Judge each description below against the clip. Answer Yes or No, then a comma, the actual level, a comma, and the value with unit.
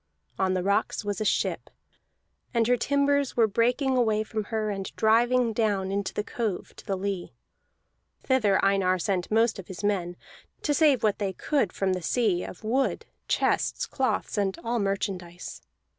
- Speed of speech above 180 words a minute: No, average, 170 wpm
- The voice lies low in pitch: No, high, 210 Hz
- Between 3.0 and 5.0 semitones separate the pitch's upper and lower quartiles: Yes, average, 3.7 semitones